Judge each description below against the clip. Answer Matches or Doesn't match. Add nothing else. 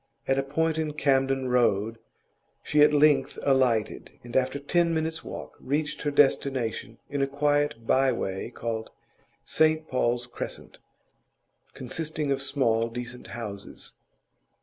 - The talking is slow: Matches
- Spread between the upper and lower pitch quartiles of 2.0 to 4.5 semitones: Matches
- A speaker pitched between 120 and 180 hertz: Matches